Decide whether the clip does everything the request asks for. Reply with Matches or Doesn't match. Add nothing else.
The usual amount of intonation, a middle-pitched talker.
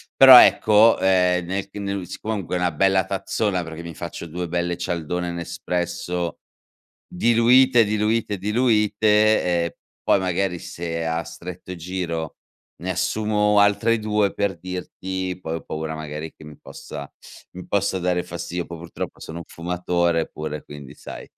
Doesn't match